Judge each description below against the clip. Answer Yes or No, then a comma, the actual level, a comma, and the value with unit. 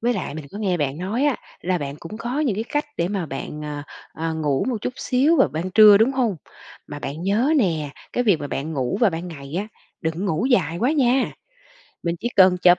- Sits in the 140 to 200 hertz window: Yes, medium, 185 Hz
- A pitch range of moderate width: No, wide, 7.0 semitones